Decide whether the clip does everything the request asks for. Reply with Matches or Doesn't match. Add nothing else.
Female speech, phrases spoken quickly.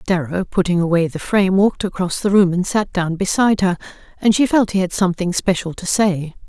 Matches